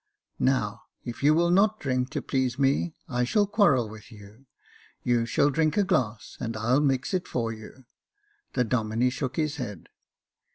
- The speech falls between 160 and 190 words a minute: Yes, average, 170 wpm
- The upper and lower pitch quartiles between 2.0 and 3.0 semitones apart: No, average, 4.3 semitones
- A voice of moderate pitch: No, low, 130 Hz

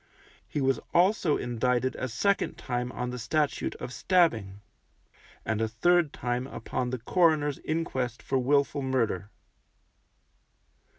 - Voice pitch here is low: Yes, low, 130 Hz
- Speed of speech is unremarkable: No, slow, 125 wpm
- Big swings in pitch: No, average, 3.9 semitones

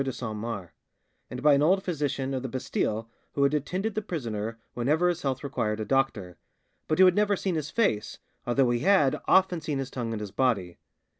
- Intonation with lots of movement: Yes, wide, 6.0 semitones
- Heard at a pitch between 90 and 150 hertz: Yes, low, 135 Hz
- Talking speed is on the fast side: Yes, fast, 210 wpm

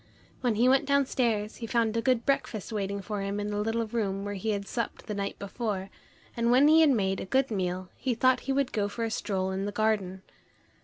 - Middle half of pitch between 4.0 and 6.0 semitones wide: No, average, 3.2 semitones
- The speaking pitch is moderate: No, high, 215 Hz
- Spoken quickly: Yes, fast, 235 wpm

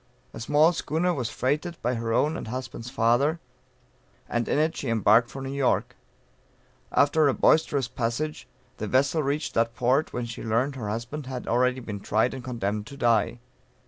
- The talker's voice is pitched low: Yes, low, 125 Hz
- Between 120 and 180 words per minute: Yes, average, 175 wpm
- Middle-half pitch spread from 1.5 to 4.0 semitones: Yes, average, 3.7 semitones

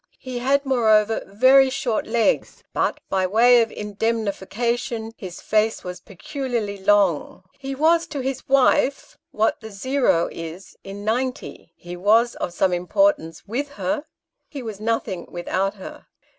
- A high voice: Yes, high, 225 Hz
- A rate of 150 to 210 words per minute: No, average, 140 wpm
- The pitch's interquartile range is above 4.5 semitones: Yes, average, 5.0 semitones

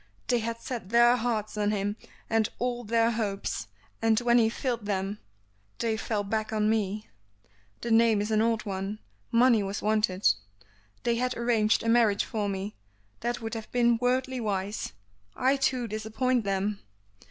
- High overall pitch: Yes, high, 220 Hz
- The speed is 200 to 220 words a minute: No, average, 165 wpm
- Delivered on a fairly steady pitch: Yes, narrow, 2.3 semitones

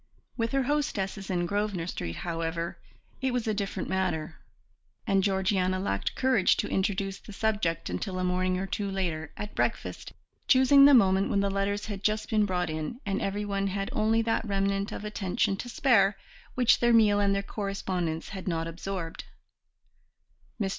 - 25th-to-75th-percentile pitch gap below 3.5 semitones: Yes, narrow, 2.5 semitones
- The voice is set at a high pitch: Yes, high, 195 Hz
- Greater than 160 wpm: Yes, average, 170 wpm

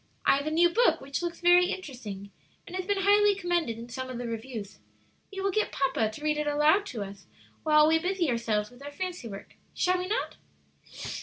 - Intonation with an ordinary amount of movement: No, wide, 7.4 semitones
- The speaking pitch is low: No, very high, 300 Hz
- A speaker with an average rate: No, fast, 215 wpm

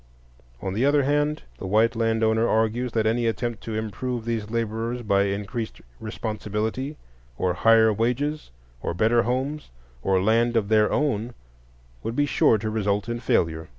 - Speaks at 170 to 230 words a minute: No, average, 160 wpm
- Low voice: Yes, low, 115 Hz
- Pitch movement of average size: No, narrow, 2.1 semitones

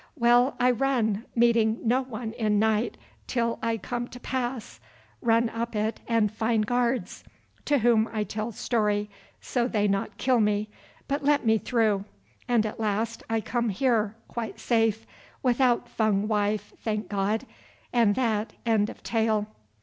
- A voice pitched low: No, high, 225 Hz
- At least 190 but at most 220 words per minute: No, average, 155 wpm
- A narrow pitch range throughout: Yes, narrow, 2.1 semitones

